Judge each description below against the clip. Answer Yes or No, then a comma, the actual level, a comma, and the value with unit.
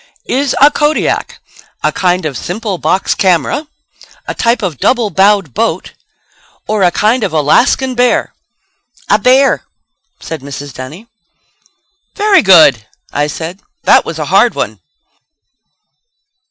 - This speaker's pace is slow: Yes, slow, 125 wpm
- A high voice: Yes, high, 195 Hz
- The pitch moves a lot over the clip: Yes, wide, 7.6 semitones